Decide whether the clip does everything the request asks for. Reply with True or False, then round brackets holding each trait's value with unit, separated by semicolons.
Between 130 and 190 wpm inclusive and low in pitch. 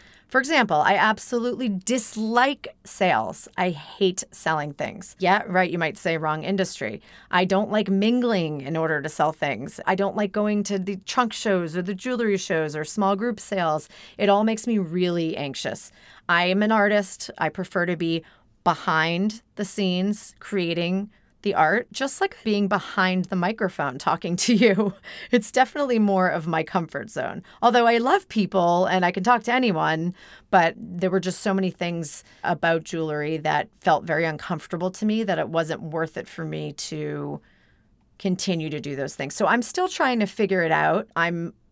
False (180 wpm; 185 Hz)